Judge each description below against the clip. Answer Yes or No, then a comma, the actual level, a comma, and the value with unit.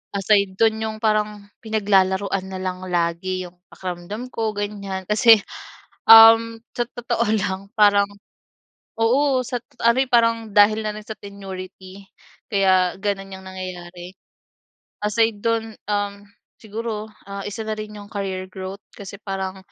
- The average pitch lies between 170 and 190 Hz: No, high, 205 Hz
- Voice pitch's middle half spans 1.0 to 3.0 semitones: Yes, narrow, 2.6 semitones